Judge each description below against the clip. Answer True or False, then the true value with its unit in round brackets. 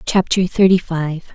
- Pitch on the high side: False (175 Hz)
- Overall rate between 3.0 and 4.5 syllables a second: True (4.2 syllables/s)